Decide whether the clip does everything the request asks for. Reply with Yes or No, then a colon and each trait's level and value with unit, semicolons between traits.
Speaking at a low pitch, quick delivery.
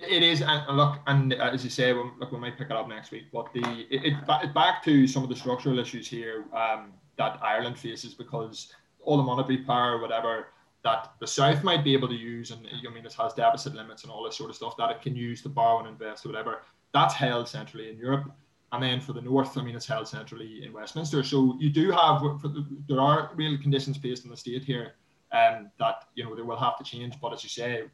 Yes: low, 125 Hz; fast, 250 wpm